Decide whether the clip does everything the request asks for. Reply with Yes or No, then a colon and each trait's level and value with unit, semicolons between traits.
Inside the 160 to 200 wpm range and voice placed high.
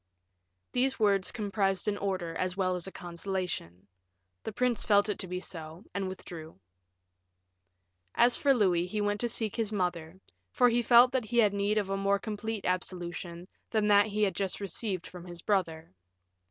Yes: average, 180 wpm; high, 195 Hz